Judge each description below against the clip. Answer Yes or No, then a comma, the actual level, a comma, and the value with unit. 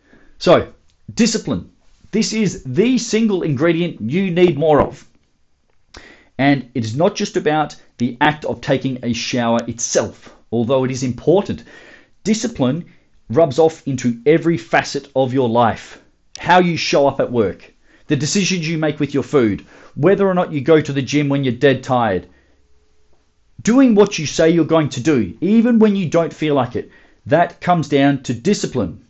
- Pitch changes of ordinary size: No, wide, 6.1 semitones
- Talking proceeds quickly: No, average, 170 wpm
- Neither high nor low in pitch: Yes, medium, 150 Hz